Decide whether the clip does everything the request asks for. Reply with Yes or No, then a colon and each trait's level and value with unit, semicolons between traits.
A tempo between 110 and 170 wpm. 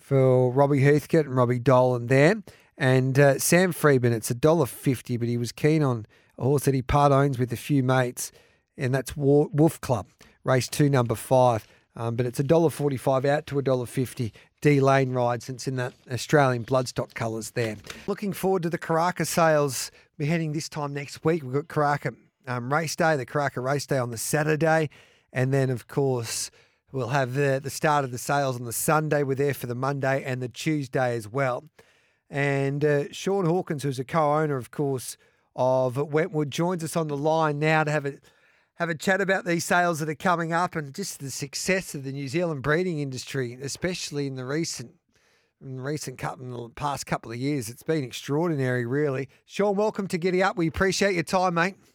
No: average, 195 wpm